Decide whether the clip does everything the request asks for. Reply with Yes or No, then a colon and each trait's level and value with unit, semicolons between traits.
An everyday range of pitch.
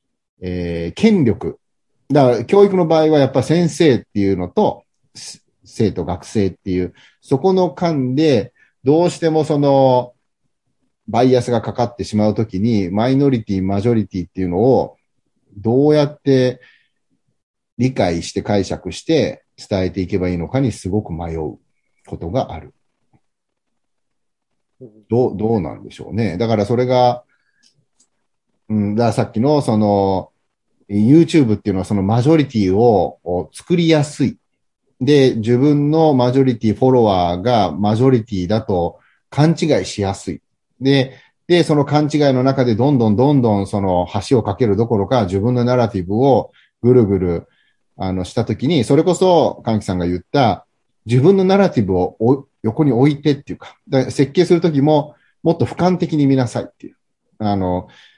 No: wide, 6.0 semitones